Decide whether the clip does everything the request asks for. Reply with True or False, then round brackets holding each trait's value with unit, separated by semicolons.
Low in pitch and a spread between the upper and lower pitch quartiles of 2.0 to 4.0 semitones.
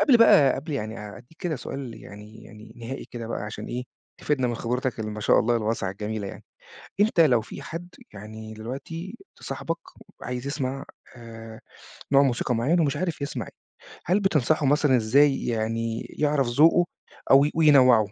False (125 Hz; 4.7 semitones)